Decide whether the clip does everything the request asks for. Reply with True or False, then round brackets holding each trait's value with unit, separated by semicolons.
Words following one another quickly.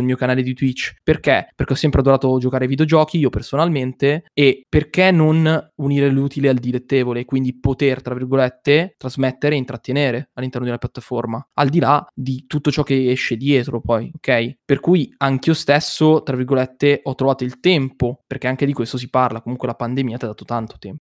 True (195 wpm)